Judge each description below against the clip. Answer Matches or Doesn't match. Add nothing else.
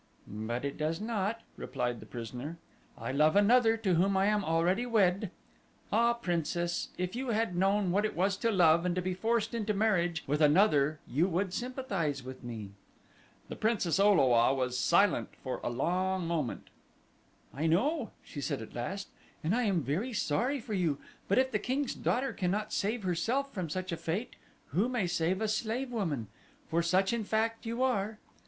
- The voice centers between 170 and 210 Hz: Matches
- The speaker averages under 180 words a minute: Doesn't match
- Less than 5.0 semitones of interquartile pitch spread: Doesn't match